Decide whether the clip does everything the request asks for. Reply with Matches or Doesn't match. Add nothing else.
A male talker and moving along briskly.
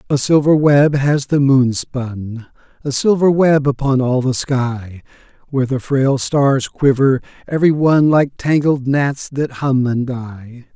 Doesn't match